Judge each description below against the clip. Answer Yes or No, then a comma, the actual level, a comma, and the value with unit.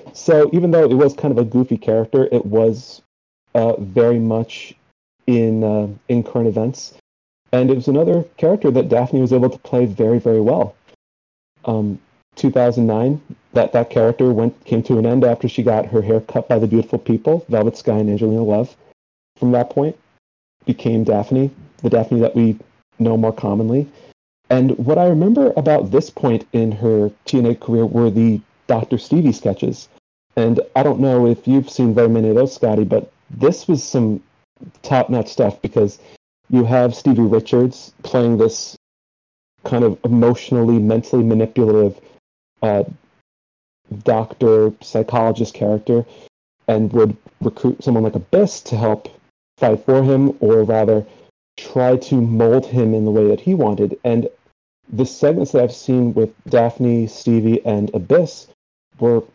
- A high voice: No, low, 115 Hz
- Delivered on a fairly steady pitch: Yes, narrow, 2.3 semitones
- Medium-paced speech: Yes, average, 160 wpm